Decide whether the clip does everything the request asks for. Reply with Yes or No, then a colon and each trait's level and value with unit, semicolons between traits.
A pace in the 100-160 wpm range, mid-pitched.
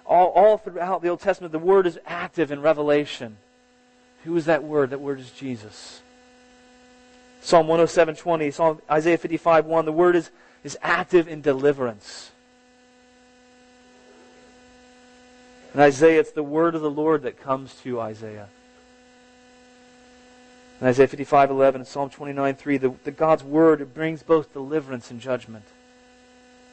Yes: average, 140 wpm; medium, 165 Hz